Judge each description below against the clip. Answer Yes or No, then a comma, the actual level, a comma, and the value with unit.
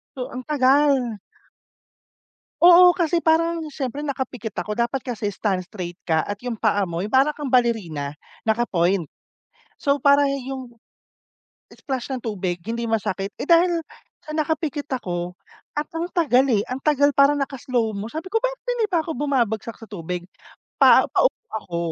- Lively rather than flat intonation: Yes, wide, 6.2 semitones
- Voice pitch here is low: No, very high, 255 Hz